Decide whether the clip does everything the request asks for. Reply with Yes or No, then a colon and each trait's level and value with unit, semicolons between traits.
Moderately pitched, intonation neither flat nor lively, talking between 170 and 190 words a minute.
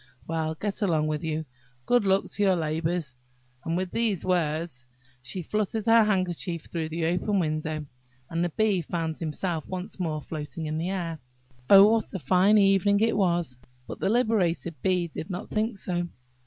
Yes: medium, 175 Hz; average, 3.6 semitones; average, 175 wpm